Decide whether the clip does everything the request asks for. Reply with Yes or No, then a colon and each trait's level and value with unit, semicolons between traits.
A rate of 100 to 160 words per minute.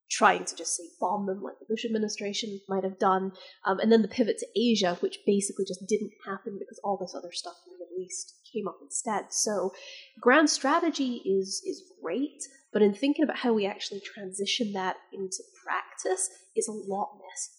No: average, 200 wpm